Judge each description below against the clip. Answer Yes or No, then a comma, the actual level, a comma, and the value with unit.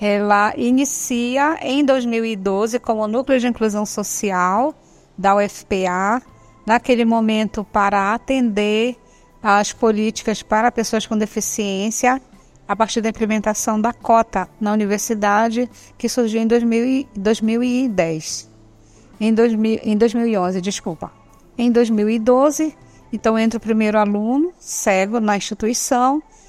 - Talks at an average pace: No, slow, 110 wpm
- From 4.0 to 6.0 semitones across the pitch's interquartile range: No, narrow, 2.5 semitones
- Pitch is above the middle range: Yes, high, 220 Hz